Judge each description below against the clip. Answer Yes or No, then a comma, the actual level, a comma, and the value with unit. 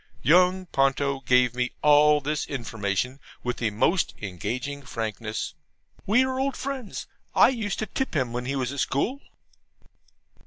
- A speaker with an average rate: Yes, average, 150 wpm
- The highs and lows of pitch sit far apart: Yes, wide, 6.9 semitones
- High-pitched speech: No, medium, 140 Hz